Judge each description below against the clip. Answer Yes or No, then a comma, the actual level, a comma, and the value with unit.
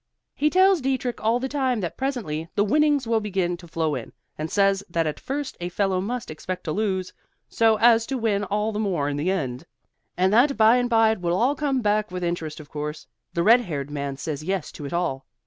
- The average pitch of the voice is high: Yes, high, 200 Hz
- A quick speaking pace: Yes, fast, 230 wpm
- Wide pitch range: Yes, wide, 6.3 semitones